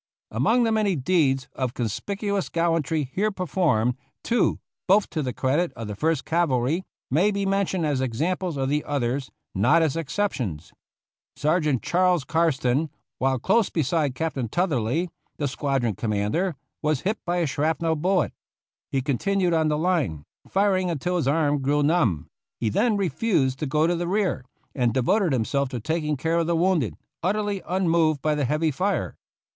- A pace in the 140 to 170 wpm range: Yes, average, 165 wpm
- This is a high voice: No, medium, 155 Hz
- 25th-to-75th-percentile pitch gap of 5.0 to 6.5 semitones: Yes, wide, 5.4 semitones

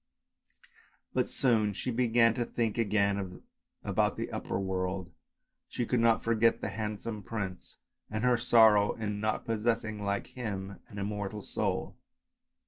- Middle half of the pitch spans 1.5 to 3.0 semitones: Yes, narrow, 2.4 semitones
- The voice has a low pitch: Yes, low, 105 Hz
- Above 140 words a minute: No, slow, 135 wpm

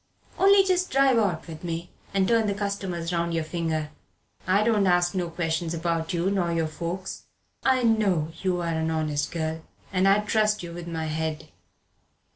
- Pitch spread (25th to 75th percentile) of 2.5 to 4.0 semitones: Yes, average, 3.7 semitones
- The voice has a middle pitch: Yes, medium, 175 Hz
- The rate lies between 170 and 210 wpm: Yes, average, 175 wpm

